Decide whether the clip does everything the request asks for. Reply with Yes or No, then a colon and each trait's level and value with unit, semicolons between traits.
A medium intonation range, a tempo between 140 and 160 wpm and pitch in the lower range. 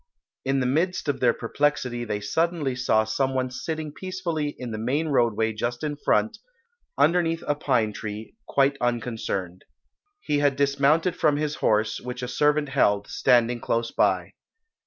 Yes: average, 4.2 semitones; average, 155 wpm; low, 130 Hz